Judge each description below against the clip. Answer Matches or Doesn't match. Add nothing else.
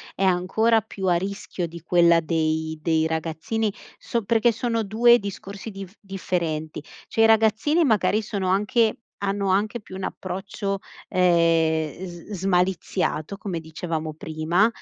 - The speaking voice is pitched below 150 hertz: Doesn't match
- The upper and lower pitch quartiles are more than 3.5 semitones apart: Matches